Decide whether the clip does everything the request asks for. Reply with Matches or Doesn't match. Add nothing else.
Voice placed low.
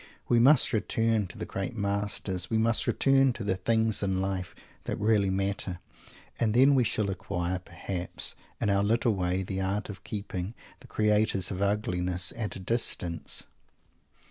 Matches